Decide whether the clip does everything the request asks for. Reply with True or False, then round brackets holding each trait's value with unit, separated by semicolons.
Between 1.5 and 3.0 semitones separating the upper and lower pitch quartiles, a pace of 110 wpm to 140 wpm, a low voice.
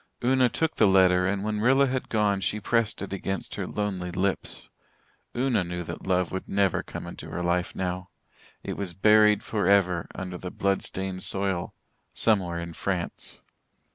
False (2.7 semitones; 170 wpm; 95 Hz)